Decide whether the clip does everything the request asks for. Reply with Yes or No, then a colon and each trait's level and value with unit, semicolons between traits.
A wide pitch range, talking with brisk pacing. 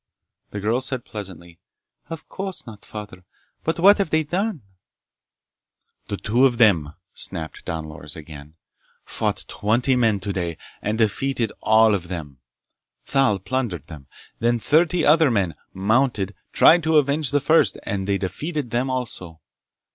No: wide, 6.7 semitones; average, 145 wpm